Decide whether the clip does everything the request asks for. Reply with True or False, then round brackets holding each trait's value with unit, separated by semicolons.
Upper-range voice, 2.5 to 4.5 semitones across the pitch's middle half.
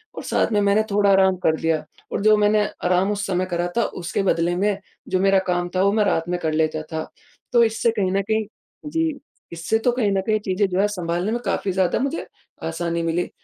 True (195 Hz; 3.2 semitones)